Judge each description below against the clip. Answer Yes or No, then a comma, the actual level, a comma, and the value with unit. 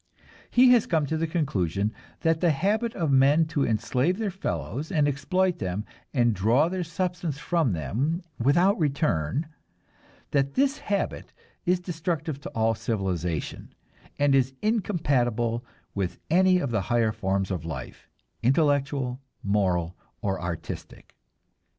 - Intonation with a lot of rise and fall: Yes, wide, 7.8 semitones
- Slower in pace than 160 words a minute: Yes, slow, 135 wpm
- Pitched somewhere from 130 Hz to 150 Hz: Yes, medium, 140 Hz